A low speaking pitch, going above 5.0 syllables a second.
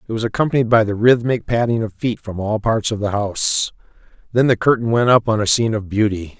Yes: low, 110 Hz; 6.0 syllables/s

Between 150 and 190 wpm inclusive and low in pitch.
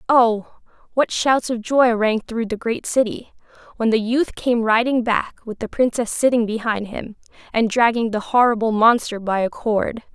No: average, 175 wpm; high, 230 Hz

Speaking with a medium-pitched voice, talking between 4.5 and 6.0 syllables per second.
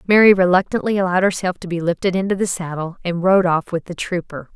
No: medium, 180 Hz; 6.3 syllables/s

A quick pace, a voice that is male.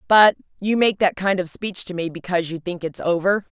No: fast, 235 wpm; female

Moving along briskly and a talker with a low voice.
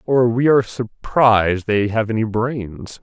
No: average, 160 wpm; low, 115 Hz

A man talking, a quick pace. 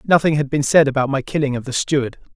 Yes: male; fast, 255 wpm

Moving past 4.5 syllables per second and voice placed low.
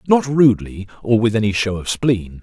Yes: 5.2 syllables/s; low, 115 Hz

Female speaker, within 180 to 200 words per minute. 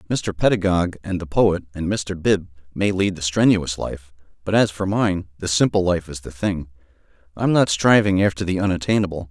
No: male; average, 185 wpm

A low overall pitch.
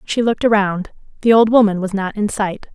No: high, 205 Hz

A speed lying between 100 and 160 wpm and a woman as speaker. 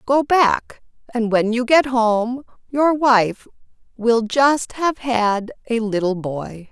Yes: average, 145 wpm; female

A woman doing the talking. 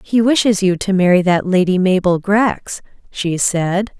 Yes: female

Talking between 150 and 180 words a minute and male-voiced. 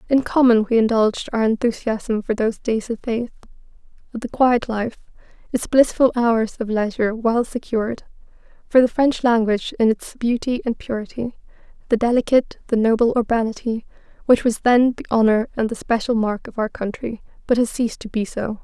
No: average, 175 wpm; female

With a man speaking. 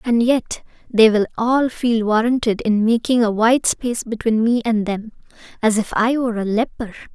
No: female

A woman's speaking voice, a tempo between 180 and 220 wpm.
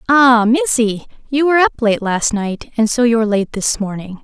Yes: female; average, 200 wpm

